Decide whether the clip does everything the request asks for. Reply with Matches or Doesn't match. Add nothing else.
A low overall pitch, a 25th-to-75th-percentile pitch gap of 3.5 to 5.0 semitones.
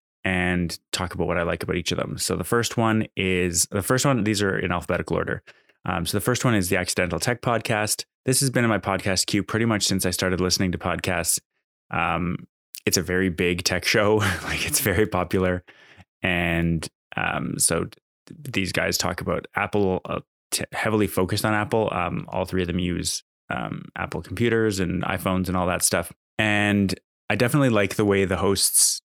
Doesn't match